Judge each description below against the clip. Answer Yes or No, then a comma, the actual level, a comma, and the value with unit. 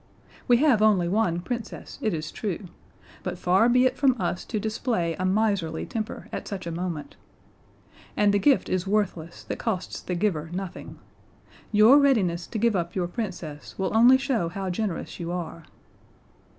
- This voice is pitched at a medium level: No, high, 195 Hz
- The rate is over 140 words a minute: Yes, average, 170 wpm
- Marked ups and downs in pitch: No, average, 4.4 semitones